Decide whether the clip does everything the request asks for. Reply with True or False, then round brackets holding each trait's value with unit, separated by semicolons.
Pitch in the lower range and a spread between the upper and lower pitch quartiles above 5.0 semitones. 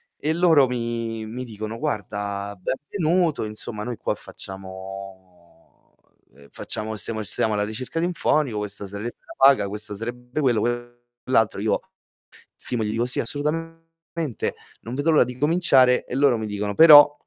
True (115 Hz; 5.5 semitones)